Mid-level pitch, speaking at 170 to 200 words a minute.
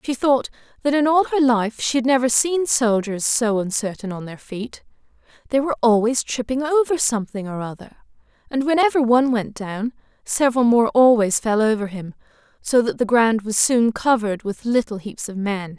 No: high, 235 Hz; average, 180 wpm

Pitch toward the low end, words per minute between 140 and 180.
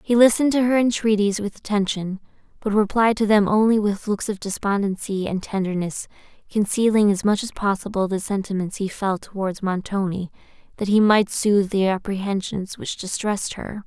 No: high, 205 Hz; average, 165 wpm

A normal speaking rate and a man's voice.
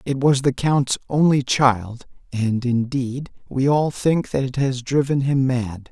Yes: average, 170 wpm; male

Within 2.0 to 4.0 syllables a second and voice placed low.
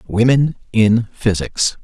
Yes: 3.6 syllables/s; low, 115 Hz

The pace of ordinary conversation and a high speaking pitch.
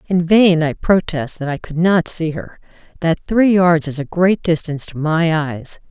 No: average, 195 wpm; medium, 165 Hz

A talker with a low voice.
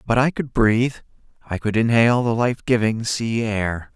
Yes: low, 115 Hz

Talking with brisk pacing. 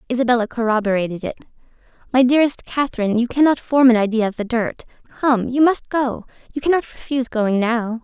No: average, 170 wpm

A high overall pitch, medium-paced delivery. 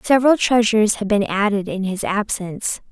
Yes: high, 210 Hz; average, 165 wpm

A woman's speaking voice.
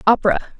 Yes: female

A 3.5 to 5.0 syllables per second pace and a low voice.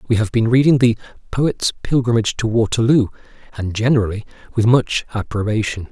No: 5.8 syllables/s; low, 115 Hz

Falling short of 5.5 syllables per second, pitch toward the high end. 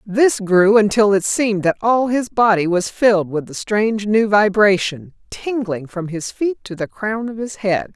Yes: 4.5 syllables/s; high, 210 Hz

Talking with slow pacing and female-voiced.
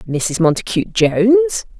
Yes: slow, 100 wpm; female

